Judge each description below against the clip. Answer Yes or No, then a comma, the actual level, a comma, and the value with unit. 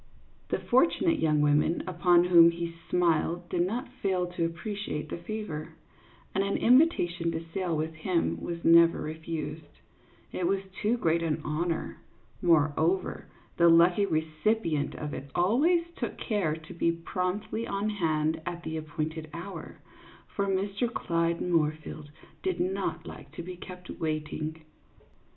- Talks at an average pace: Yes, average, 145 wpm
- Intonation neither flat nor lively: Yes, average, 3.4 semitones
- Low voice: No, medium, 170 Hz